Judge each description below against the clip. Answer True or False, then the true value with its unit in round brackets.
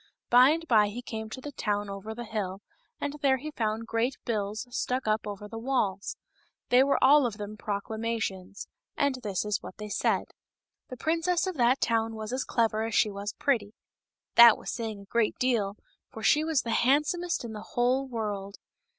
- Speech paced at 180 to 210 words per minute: True (195 wpm)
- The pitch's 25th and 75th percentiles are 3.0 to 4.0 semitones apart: True (3.7 semitones)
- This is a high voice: True (225 Hz)